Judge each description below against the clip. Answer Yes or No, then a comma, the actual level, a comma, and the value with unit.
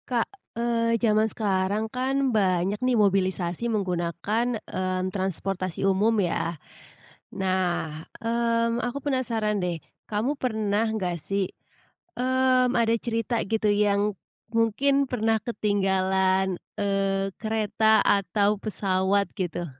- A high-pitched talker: Yes, high, 210 Hz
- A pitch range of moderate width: Yes, average, 3.4 semitones